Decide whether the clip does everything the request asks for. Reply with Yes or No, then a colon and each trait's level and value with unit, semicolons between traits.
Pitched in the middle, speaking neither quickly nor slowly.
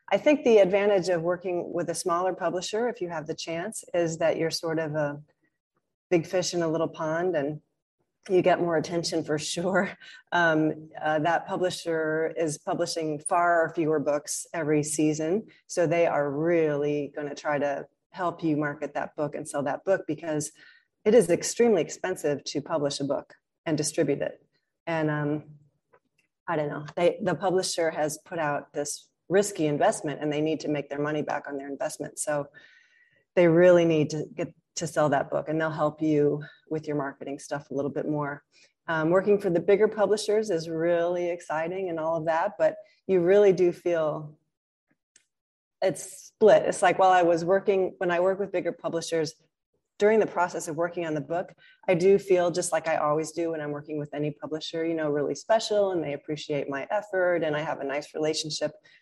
Yes: medium, 165 Hz; average, 195 wpm